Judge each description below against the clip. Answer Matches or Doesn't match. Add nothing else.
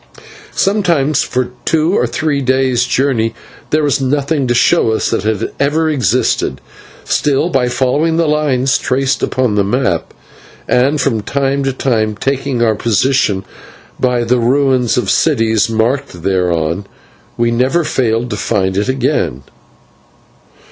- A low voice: Matches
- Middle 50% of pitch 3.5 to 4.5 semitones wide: Matches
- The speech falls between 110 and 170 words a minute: Matches